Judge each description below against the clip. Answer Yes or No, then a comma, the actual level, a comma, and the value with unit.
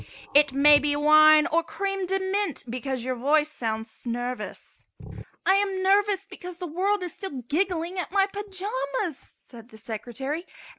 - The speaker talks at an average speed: Yes, average, 155 wpm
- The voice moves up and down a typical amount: No, wide, 6.4 semitones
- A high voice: Yes, very high, 310 Hz